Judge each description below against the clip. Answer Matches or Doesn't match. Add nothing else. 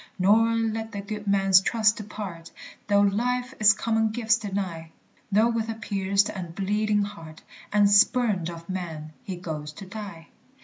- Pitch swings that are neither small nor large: Matches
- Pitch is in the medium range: Doesn't match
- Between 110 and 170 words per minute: Matches